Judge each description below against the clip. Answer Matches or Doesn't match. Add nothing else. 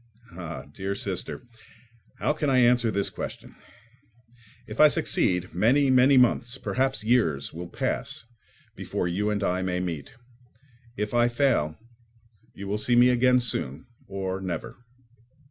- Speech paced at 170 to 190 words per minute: Doesn't match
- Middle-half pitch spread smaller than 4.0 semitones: Doesn't match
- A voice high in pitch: Doesn't match